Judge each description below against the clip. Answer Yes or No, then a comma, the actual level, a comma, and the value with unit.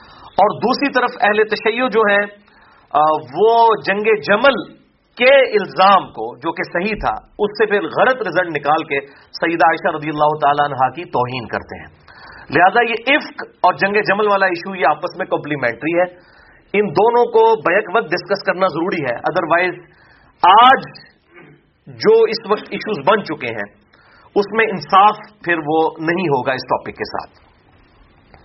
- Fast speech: No, average, 160 wpm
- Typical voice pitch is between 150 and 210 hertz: Yes, medium, 185 Hz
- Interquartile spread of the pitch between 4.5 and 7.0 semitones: Yes, wide, 5.6 semitones